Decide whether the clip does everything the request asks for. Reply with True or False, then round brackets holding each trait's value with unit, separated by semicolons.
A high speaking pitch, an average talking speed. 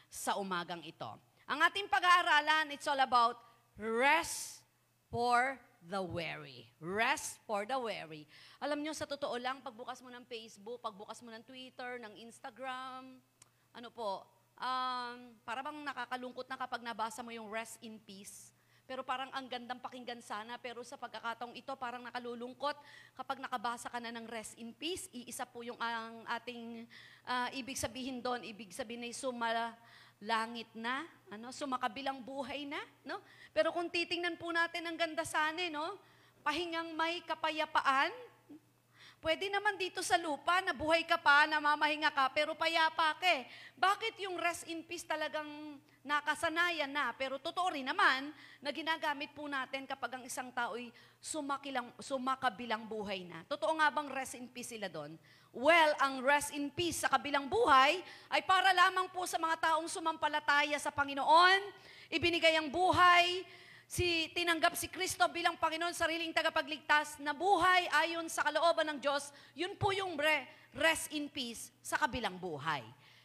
False (280 Hz; 160 wpm)